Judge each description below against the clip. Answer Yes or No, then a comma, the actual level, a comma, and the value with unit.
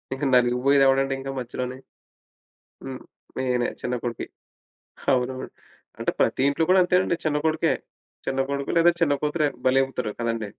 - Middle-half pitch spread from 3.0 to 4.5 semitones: No, narrow, 2.6 semitones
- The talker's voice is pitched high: No, low, 135 Hz